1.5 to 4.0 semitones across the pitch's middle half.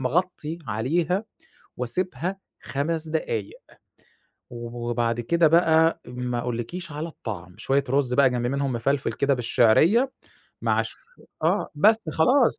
No: wide, 5.6 semitones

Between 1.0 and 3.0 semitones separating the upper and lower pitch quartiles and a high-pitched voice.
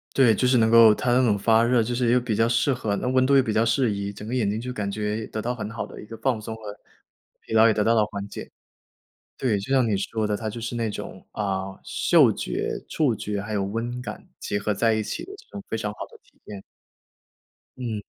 No: narrow, 2.6 semitones; low, 110 Hz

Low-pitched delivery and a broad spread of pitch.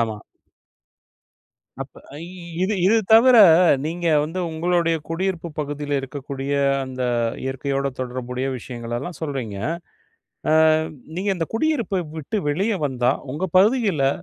No: medium, 150 Hz; wide, 5.9 semitones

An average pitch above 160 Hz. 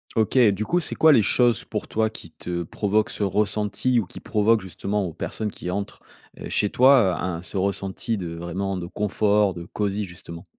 No: low, 100 Hz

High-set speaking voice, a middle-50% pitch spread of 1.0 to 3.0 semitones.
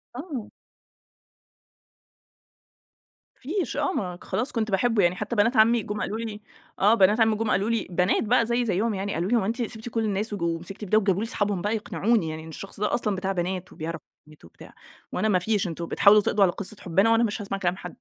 No: high, 205 Hz; average, 3.4 semitones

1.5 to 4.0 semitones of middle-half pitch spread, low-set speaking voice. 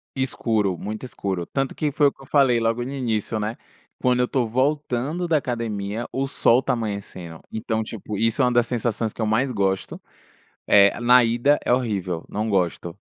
Yes: average, 3.6 semitones; low, 115 Hz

